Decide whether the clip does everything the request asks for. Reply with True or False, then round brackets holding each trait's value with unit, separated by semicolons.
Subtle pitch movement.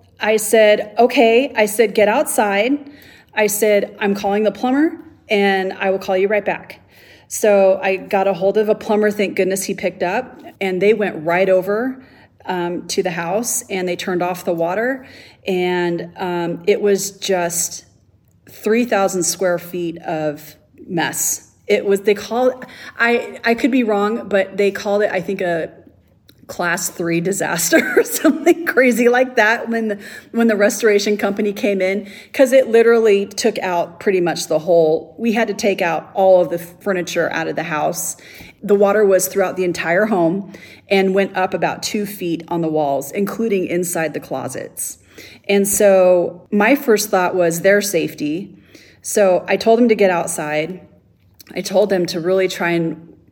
False (3.4 semitones)